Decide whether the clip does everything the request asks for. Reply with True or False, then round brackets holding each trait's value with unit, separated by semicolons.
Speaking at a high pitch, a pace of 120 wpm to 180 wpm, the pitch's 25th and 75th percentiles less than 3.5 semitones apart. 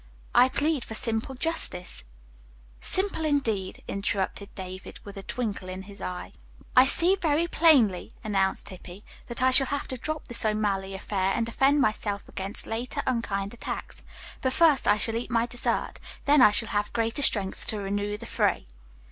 False (220 Hz; 170 wpm; 4.8 semitones)